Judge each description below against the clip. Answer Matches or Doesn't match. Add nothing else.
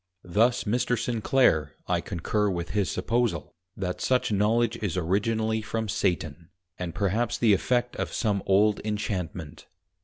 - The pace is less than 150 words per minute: Matches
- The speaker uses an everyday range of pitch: Matches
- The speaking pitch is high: Doesn't match